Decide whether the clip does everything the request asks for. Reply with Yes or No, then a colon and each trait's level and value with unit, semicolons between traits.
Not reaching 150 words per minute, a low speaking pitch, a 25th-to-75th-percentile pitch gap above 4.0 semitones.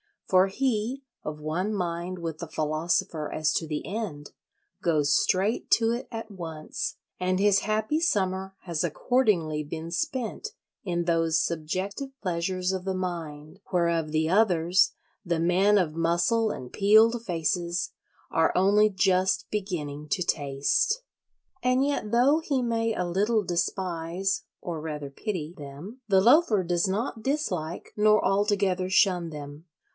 No: average, 140 wpm; medium, 185 Hz; average, 4.4 semitones